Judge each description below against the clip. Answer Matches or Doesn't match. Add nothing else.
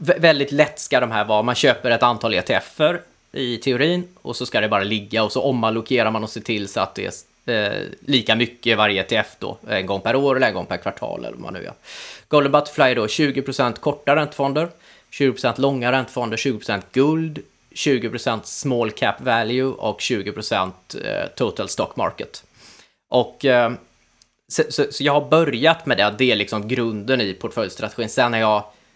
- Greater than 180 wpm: Matches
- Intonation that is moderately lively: Matches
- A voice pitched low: Matches